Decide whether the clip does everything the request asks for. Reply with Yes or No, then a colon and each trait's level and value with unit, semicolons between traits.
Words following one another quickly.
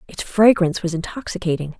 No: slow, 135 wpm